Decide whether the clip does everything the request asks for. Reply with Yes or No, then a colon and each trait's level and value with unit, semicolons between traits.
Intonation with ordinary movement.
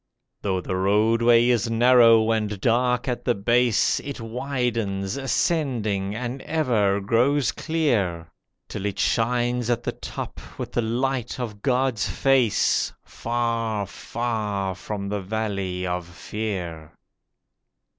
Yes: average, 3.6 semitones